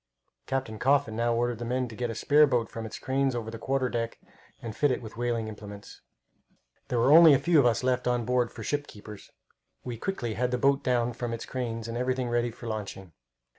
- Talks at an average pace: No, fast, 225 wpm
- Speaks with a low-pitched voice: Yes, low, 120 Hz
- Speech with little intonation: Yes, narrow, 2.2 semitones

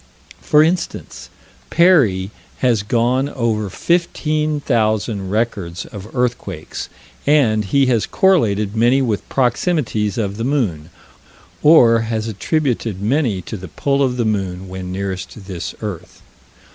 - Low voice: Yes, low, 115 Hz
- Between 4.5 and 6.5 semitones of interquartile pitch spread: Yes, wide, 5.5 semitones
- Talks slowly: Yes, slow, 120 wpm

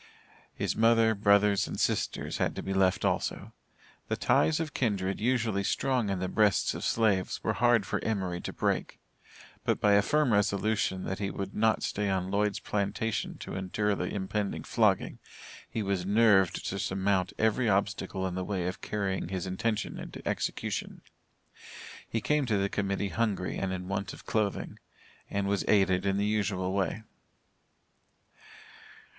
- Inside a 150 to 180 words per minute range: Yes, average, 160 wpm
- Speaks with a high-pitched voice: No, low, 100 Hz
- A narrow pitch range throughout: Yes, narrow, 2.2 semitones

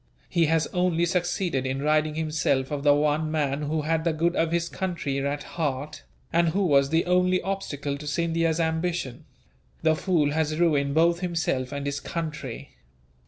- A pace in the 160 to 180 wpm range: Yes, average, 170 wpm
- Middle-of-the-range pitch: Yes, medium, 160 Hz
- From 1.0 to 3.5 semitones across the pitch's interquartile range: Yes, average, 2.8 semitones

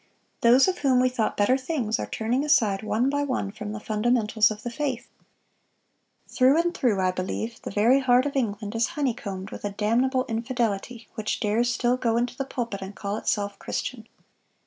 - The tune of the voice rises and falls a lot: No, average, 3.5 semitones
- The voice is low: No, high, 235 Hz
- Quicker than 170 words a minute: Yes, average, 190 wpm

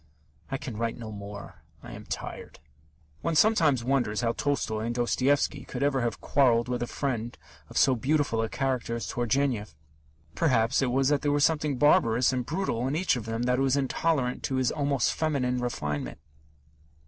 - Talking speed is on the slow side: No, average, 180 wpm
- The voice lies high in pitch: No, low, 125 Hz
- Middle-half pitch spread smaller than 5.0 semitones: Yes, average, 3.4 semitones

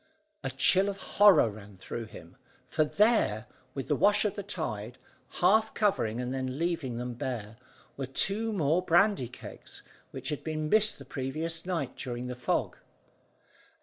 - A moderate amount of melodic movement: No, wide, 7.8 semitones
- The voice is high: No, medium, 150 Hz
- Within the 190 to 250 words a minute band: No, average, 160 wpm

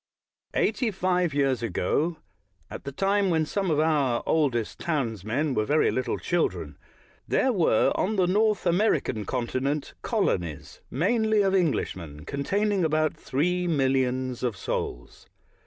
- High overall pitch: No, medium, 155 Hz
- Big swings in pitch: Yes, wide, 6.3 semitones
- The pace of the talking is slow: Yes, slow, 130 wpm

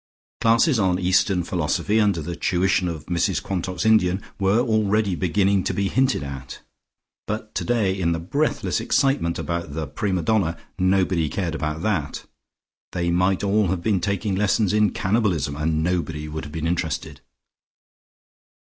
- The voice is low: Yes, very low, 95 Hz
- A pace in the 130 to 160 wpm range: Yes, average, 150 wpm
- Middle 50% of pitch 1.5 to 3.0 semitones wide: No, average, 3.7 semitones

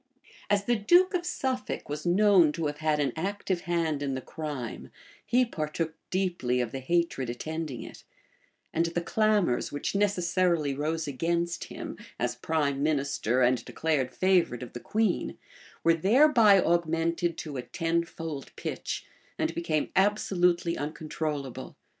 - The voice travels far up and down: No, average, 4.2 semitones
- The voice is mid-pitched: Yes, medium, 165 Hz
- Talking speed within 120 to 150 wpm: Yes, average, 140 wpm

